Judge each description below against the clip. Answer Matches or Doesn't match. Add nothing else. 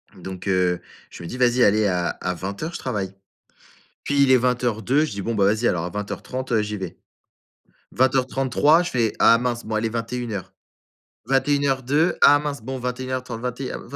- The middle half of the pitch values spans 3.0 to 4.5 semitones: Matches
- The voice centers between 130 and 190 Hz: Doesn't match